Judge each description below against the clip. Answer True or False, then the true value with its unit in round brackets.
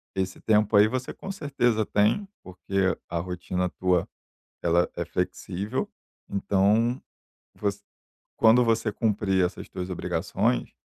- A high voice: False (100 Hz)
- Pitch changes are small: False (3.6 semitones)